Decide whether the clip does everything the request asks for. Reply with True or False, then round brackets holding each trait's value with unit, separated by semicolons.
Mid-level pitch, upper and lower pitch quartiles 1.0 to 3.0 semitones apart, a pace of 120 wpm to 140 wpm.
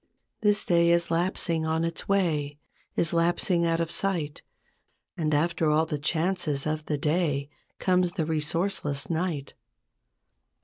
True (165 Hz; 2.4 semitones; 135 wpm)